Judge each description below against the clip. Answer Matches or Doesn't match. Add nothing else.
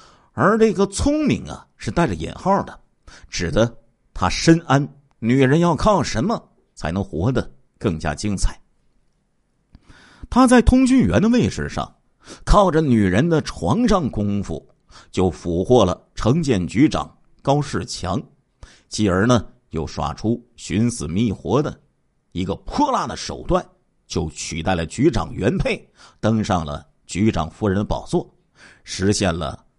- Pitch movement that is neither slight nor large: Doesn't match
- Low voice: Matches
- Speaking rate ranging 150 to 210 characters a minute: Matches